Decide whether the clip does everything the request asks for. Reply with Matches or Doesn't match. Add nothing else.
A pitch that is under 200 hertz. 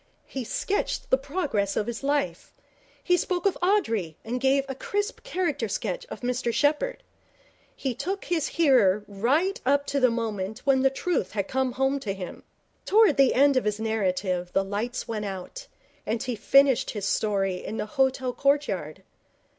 Doesn't match